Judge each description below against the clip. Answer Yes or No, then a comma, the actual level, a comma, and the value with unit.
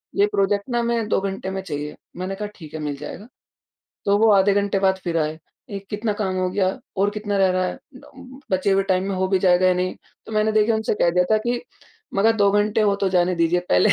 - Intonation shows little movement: Yes, narrow, 2.2 semitones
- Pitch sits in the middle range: No, high, 195 Hz